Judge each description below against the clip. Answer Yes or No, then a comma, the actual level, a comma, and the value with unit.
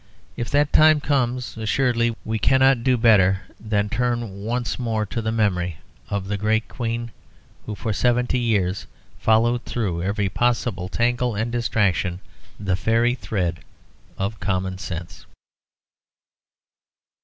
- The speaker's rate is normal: No, slow, 130 wpm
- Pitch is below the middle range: Yes, low, 110 Hz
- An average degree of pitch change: Yes, average, 3.6 semitones